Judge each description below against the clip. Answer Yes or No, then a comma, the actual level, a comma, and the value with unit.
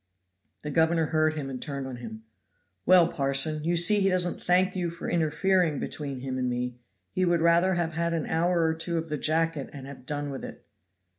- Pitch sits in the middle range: Yes, medium, 160 Hz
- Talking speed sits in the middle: No, fast, 210 wpm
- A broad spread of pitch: No, average, 3.7 semitones